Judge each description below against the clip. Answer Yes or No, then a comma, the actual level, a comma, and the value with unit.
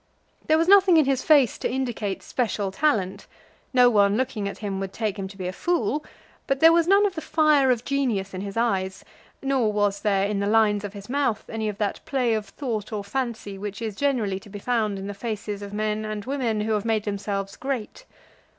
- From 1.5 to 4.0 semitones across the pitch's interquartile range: No, average, 4.7 semitones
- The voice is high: Yes, high, 215 Hz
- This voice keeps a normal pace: No, fast, 225 wpm